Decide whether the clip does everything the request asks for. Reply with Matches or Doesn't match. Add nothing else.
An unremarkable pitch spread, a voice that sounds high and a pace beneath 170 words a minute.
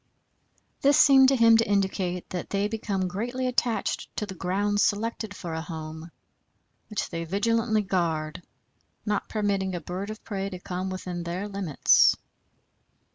Matches